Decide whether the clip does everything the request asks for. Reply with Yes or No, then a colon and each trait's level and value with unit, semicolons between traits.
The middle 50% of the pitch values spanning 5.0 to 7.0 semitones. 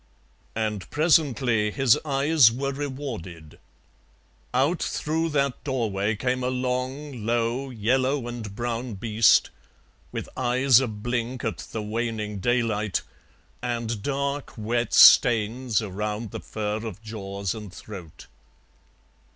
No: average, 3.6 semitones